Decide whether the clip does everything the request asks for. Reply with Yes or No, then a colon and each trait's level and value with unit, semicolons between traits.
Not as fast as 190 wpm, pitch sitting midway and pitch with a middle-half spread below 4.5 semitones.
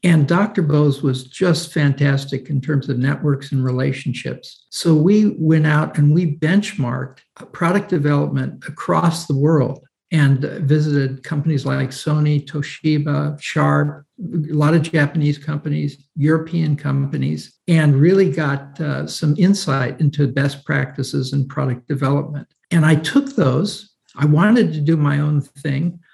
Yes: average, 140 wpm; medium, 150 Hz; narrow, 2.4 semitones